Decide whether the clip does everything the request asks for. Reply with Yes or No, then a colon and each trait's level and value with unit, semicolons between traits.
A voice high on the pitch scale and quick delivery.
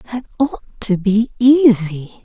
No: high, 225 Hz; slow, 135 wpm